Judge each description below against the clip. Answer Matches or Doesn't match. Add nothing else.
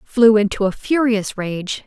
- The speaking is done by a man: Doesn't match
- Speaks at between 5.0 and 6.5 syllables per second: Doesn't match